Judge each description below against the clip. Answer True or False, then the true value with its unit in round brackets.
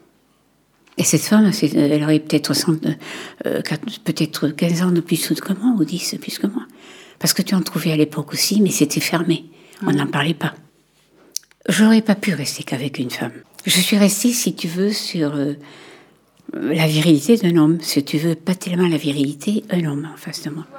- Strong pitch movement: False (3.7 semitones)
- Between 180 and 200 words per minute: True (190 wpm)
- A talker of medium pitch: True (165 Hz)